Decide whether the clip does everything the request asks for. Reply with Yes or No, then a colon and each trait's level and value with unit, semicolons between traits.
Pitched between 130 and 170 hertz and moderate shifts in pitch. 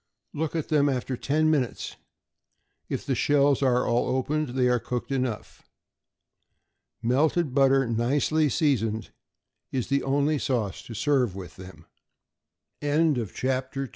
Yes: low, 135 Hz; average, 3.1 semitones